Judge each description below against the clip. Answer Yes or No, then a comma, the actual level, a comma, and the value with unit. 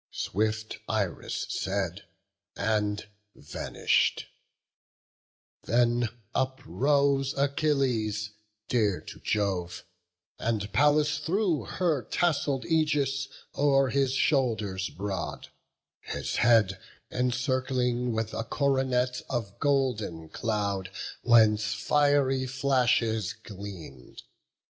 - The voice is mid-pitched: No, low, 120 Hz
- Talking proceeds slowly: Yes, slow, 80 wpm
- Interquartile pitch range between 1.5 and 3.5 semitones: No, average, 4.5 semitones